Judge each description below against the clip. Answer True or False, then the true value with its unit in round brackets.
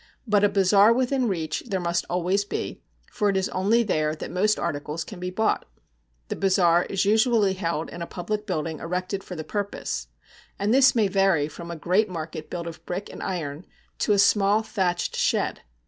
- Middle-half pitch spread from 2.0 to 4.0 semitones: True (3.4 semitones)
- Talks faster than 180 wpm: True (195 wpm)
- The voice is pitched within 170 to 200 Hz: True (190 Hz)